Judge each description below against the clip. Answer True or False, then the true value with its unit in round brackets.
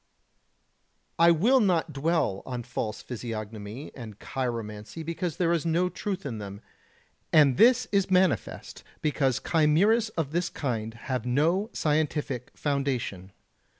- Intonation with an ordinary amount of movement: False (6.1 semitones)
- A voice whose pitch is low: False (150 Hz)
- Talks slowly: True (125 wpm)